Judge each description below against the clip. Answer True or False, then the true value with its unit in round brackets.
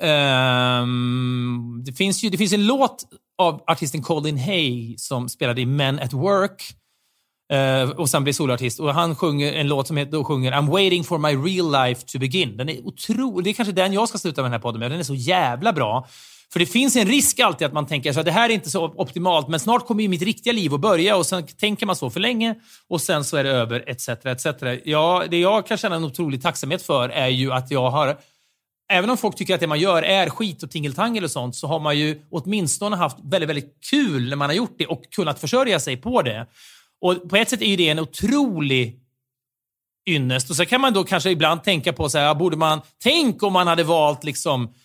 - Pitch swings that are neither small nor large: False (5.9 semitones)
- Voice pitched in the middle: True (160 Hz)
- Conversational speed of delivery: False (240 wpm)